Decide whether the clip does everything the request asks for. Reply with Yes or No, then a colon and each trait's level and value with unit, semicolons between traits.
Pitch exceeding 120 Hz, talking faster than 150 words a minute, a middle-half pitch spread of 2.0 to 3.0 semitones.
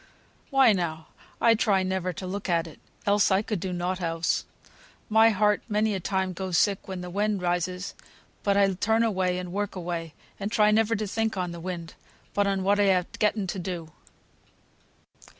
Yes: high, 190 Hz; average, 190 wpm; narrow, 2.6 semitones